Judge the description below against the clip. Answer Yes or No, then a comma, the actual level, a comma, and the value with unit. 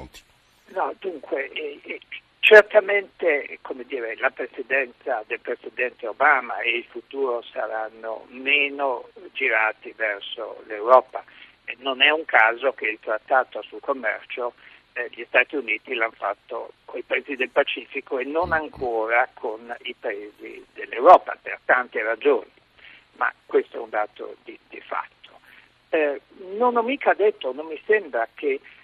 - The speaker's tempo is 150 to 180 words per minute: No, average, 135 wpm